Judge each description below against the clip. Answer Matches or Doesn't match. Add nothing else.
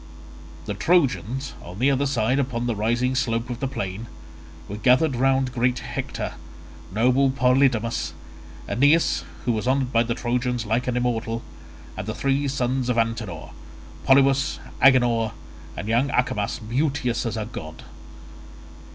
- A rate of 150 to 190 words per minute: Doesn't match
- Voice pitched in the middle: Doesn't match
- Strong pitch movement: Doesn't match